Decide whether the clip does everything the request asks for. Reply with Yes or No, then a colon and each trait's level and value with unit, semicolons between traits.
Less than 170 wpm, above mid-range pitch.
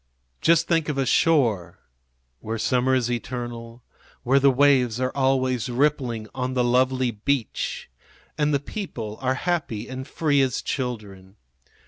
No: average, 140 wpm; low, 130 Hz